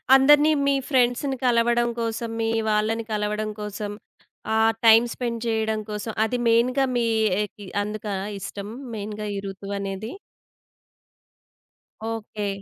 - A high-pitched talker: Yes, high, 220 Hz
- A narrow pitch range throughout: Yes, narrow, 2.2 semitones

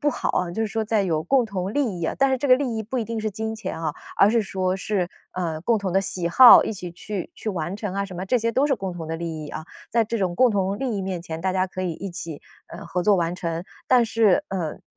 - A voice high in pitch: Yes, high, 195 Hz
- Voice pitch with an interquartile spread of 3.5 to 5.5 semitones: Yes, average, 4.2 semitones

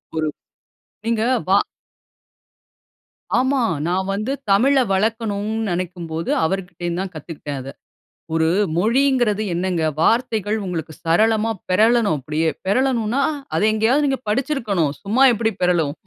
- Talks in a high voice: Yes, high, 205 Hz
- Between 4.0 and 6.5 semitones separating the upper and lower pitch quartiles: Yes, average, 5.0 semitones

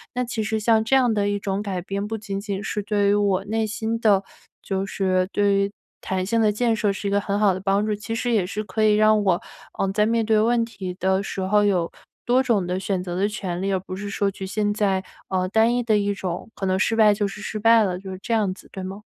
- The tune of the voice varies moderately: No, narrow, 2.2 semitones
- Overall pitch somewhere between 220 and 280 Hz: No, high, 205 Hz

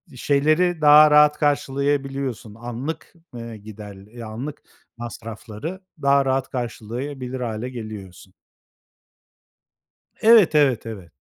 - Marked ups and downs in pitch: No, average, 4.8 semitones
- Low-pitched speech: Yes, low, 130 Hz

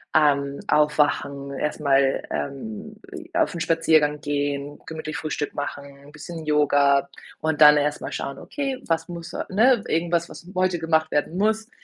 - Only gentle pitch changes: No, average, 3.2 semitones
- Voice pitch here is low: No, medium, 155 Hz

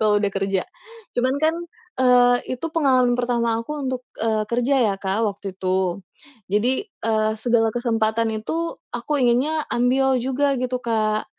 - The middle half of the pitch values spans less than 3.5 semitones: Yes, average, 2.9 semitones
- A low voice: No, high, 240 Hz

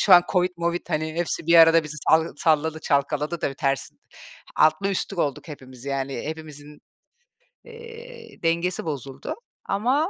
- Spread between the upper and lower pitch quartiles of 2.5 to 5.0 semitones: Yes, average, 3.5 semitones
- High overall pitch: No, medium, 160 Hz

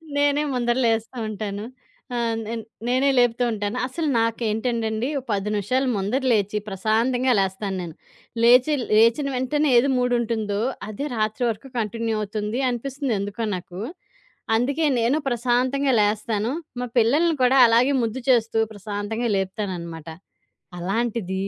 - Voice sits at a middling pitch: No, high, 230 Hz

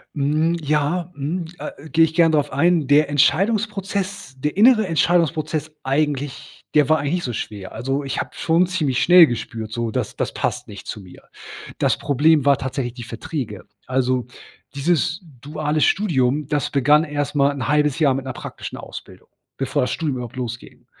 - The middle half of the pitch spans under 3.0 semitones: No, average, 3.7 semitones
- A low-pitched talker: No, medium, 145 Hz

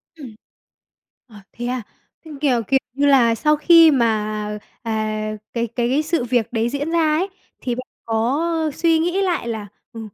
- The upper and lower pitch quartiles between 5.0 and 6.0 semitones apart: Yes, wide, 5.4 semitones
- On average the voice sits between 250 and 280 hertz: Yes, very high, 255 Hz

